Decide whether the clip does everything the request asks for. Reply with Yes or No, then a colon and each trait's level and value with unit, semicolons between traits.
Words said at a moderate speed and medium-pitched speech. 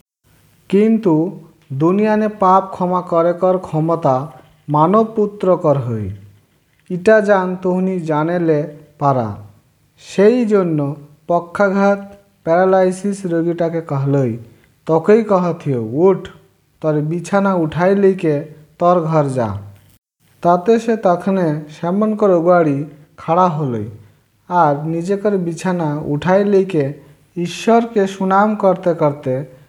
No: slow, 95 wpm; medium, 170 Hz